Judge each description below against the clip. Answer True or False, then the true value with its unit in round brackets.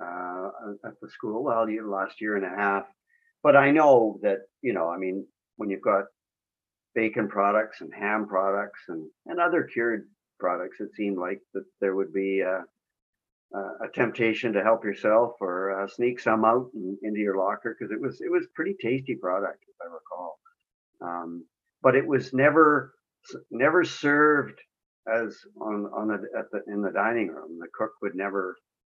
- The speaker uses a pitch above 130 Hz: False (105 Hz)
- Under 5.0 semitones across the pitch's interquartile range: False (5.3 semitones)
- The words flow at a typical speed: True (180 wpm)